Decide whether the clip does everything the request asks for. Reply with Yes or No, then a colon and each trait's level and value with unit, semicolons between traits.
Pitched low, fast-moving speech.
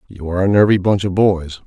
Yes: very low, 95 Hz; fast, 250 wpm